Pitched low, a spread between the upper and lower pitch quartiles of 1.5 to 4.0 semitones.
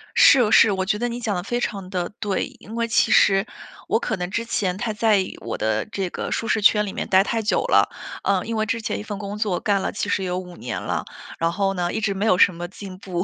No: high, 200 Hz; average, 2.9 semitones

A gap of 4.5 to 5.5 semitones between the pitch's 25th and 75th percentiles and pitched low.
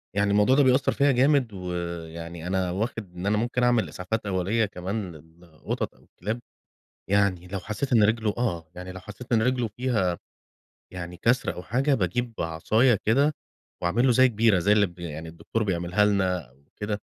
Yes: average, 4.8 semitones; low, 100 Hz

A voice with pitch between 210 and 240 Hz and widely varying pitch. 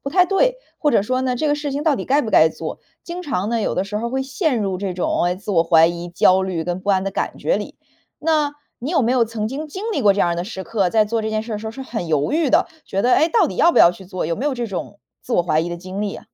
Yes: high, 220 Hz; wide, 7.2 semitones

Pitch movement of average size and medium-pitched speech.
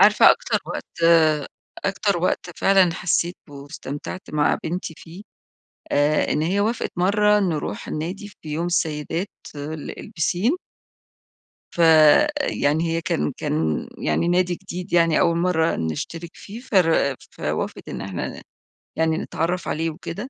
Yes: average, 3.1 semitones; medium, 165 Hz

